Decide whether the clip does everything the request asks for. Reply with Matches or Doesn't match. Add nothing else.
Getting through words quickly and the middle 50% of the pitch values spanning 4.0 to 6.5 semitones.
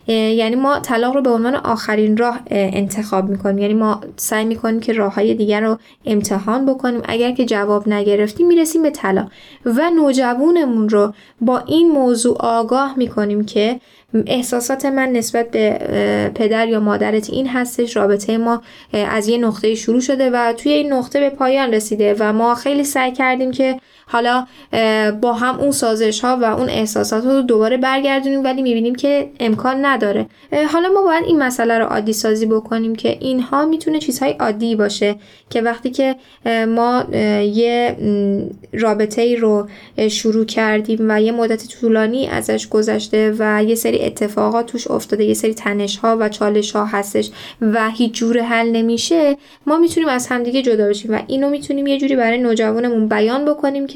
Doesn't match